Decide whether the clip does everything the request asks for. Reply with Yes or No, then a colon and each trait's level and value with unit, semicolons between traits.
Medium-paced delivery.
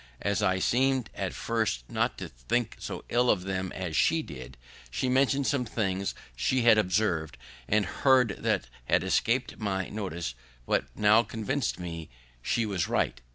Yes: average, 160 wpm